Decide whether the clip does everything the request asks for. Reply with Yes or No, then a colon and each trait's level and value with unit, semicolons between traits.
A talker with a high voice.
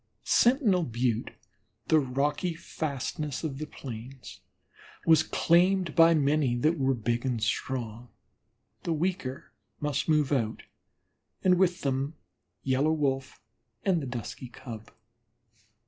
No: medium, 140 Hz